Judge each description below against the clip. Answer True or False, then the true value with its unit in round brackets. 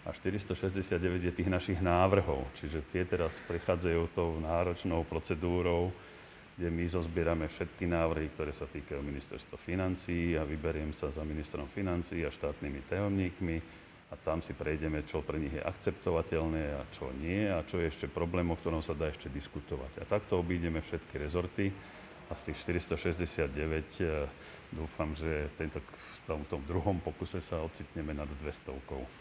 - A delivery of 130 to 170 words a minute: True (155 wpm)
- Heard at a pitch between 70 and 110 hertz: True (85 Hz)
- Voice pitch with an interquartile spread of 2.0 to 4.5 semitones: True (2.5 semitones)